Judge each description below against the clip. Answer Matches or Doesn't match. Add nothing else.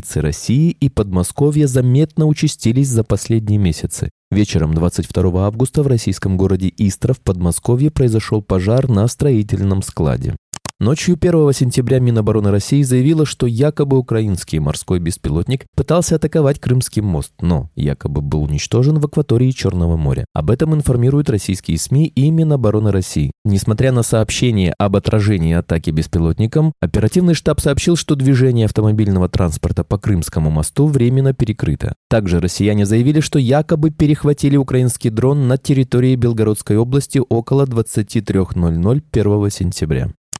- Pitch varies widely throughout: Matches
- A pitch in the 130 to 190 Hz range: Doesn't match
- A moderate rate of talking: Matches